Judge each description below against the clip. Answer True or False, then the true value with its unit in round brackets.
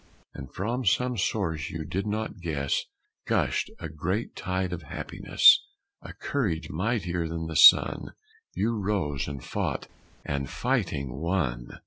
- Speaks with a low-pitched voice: True (85 Hz)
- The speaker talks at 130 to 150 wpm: True (135 wpm)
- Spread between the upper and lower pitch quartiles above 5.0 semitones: True (5.4 semitones)